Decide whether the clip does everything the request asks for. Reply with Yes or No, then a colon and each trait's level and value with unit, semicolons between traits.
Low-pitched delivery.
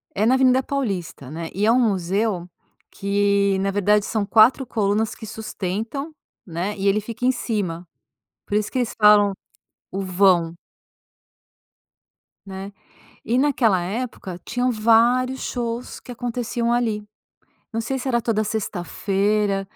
No: high, 210 Hz